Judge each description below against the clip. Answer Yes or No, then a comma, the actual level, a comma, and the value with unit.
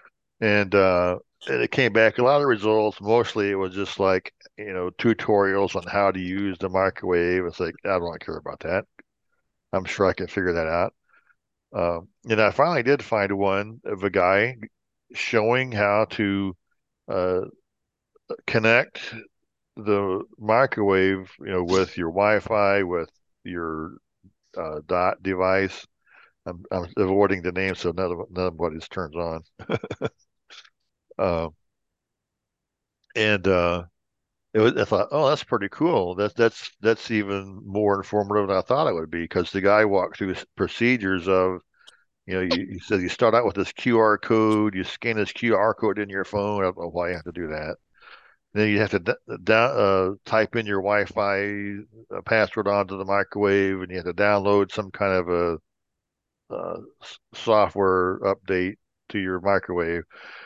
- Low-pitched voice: Yes, low, 100 Hz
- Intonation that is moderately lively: No, narrow, 2.3 semitones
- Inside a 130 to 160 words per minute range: No, average, 170 wpm